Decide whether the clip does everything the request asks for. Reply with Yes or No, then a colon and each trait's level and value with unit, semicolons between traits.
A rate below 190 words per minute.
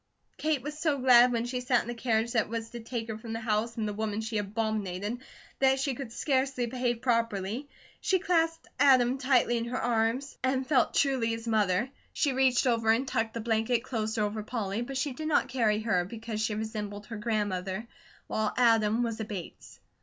No: average, 200 wpm